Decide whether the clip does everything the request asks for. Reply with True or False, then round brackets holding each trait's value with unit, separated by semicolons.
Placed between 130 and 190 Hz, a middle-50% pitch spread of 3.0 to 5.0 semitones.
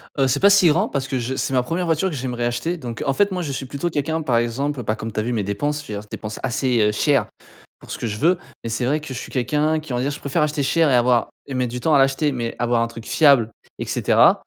True (135 Hz; 4.2 semitones)